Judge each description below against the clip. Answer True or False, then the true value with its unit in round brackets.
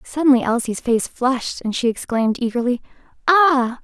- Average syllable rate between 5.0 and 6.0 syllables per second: True (5.3 syllables/s)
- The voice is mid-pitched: False (255 Hz)